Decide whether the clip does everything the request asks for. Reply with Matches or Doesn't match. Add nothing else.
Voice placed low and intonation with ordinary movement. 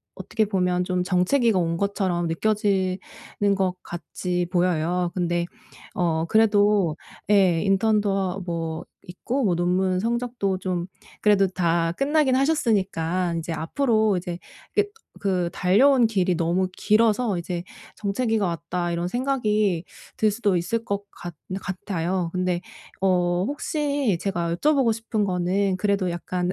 Doesn't match